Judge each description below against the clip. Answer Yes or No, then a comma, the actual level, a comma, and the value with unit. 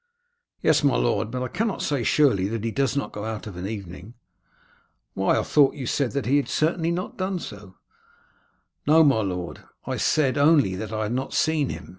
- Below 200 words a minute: No, fast, 205 wpm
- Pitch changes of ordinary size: No, wide, 5.8 semitones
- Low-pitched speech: Yes, low, 130 Hz